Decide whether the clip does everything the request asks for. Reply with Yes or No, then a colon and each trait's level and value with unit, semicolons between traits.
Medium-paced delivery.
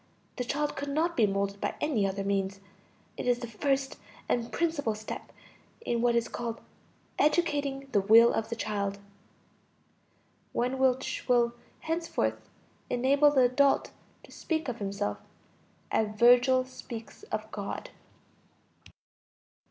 No: slow, 130 wpm